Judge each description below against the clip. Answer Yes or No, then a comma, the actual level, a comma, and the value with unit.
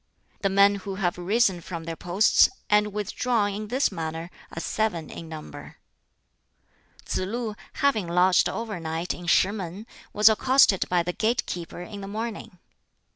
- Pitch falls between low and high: No, high, 195 Hz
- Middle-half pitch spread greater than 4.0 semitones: No, average, 3.6 semitones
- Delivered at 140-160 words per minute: Yes, average, 155 wpm